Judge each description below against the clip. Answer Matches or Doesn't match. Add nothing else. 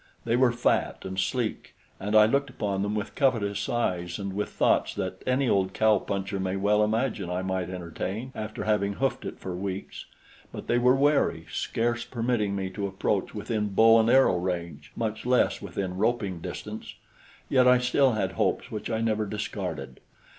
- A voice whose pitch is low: Matches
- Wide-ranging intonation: Doesn't match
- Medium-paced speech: Matches